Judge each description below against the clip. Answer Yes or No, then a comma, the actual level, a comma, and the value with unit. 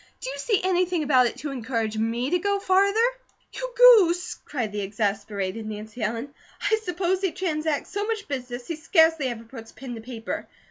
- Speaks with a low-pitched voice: No, very high, 280 Hz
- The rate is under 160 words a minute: No, average, 185 wpm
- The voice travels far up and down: Yes, wide, 8.2 semitones